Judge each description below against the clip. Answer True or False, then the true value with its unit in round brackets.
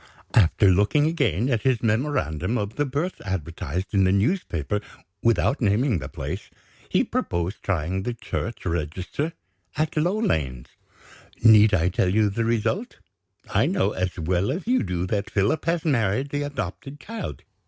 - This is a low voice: True (105 Hz)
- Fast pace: False (155 wpm)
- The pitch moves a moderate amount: False (7.7 semitones)